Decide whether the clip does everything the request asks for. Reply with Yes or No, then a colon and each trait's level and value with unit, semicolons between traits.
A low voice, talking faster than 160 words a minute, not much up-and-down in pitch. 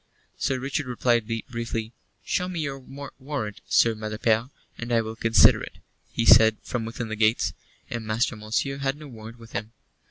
No: low, 115 Hz; average, 170 wpm; average, 3.3 semitones